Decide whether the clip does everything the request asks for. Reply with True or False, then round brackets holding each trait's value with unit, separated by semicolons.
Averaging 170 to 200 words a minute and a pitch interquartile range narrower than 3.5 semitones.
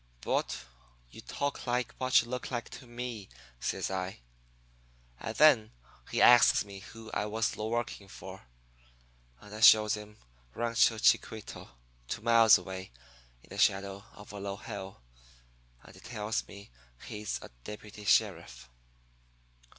False (140 wpm; 3.0 semitones)